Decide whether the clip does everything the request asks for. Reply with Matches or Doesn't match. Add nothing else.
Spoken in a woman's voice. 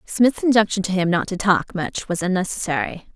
Matches